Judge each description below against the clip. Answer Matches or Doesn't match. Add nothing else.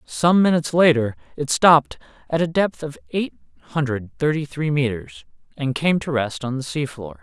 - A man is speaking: Matches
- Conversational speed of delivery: Matches